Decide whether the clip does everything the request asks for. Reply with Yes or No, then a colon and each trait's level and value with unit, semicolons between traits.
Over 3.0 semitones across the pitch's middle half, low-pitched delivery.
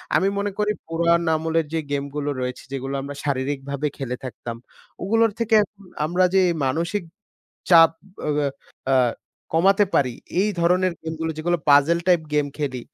No: average, 4.2 semitones; medium, 160 Hz